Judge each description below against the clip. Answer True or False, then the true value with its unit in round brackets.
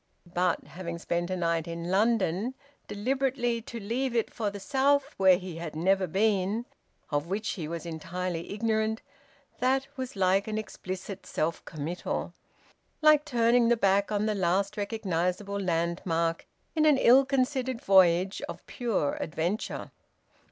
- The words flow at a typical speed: True (145 wpm)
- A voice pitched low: False (200 Hz)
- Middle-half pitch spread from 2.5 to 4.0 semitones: False (5.2 semitones)